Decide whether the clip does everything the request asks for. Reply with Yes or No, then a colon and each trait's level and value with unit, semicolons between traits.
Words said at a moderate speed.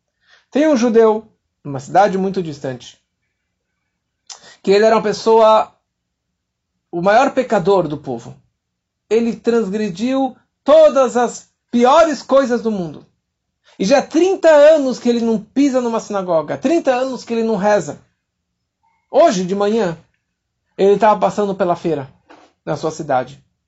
Yes: average, 135 wpm